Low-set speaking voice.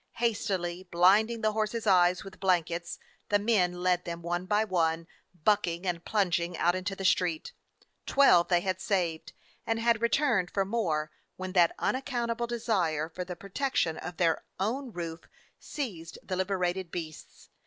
No: medium, 185 Hz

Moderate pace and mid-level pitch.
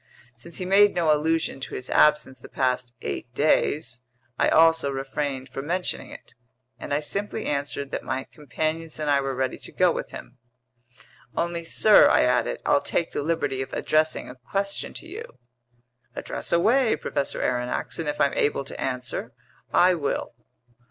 Yes: average, 170 wpm; medium, 150 Hz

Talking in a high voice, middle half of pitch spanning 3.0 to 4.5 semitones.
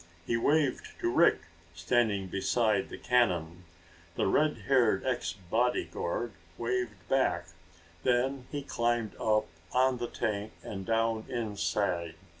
No: low, 115 Hz; average, 3.9 semitones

